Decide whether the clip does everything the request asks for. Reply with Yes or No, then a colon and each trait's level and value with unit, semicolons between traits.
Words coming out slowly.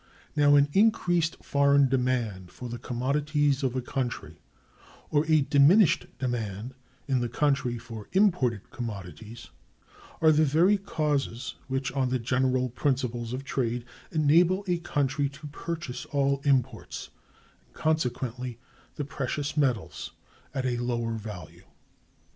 Yes: slow, 130 wpm